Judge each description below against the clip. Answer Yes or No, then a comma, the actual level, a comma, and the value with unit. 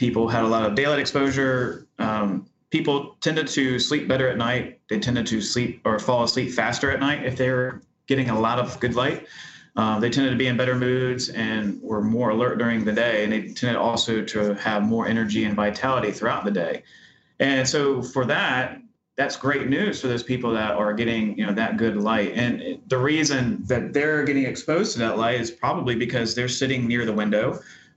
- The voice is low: Yes, low, 120 Hz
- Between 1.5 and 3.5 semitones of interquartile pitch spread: Yes, average, 2.8 semitones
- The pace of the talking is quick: Yes, fast, 210 wpm